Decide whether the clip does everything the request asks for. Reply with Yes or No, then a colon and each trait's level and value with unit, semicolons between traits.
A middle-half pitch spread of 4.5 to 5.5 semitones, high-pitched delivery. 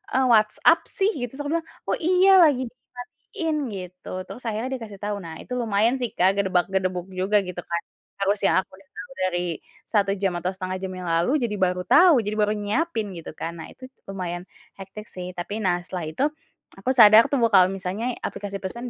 Yes: average, 4.9 semitones; high, 200 Hz